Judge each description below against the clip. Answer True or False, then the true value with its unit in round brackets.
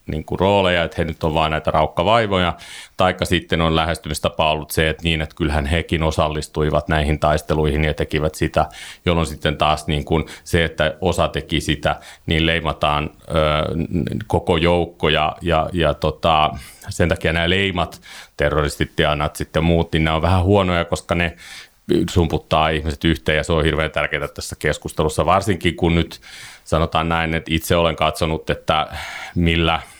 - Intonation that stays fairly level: True (1.9 semitones)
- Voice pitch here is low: True (80 Hz)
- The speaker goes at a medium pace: False (160 wpm)